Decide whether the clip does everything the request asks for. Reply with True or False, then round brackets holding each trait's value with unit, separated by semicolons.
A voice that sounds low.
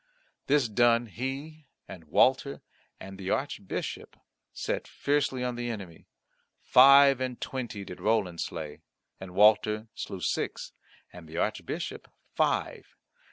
True (115 Hz)